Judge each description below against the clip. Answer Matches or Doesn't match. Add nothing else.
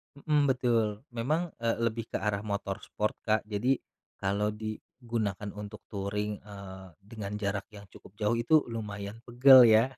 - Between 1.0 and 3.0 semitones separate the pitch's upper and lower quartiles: Matches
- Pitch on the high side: Doesn't match